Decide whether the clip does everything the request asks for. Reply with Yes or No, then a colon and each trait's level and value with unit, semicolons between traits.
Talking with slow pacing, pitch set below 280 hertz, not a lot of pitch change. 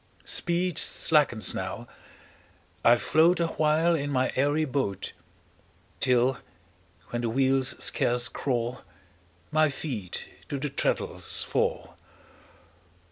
No: slow, 100 wpm; low, 135 Hz; average, 4.3 semitones